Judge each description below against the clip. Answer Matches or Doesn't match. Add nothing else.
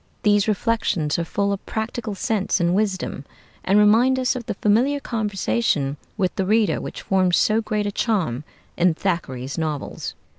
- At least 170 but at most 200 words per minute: Doesn't match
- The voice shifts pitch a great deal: Doesn't match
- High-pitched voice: Matches